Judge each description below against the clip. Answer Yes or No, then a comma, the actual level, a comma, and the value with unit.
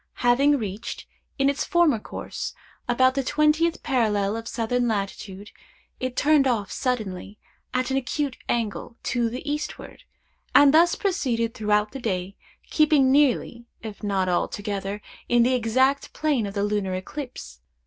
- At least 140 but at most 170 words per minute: Yes, average, 145 wpm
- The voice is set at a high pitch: Yes, high, 240 Hz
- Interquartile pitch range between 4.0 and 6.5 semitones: Yes, average, 4.9 semitones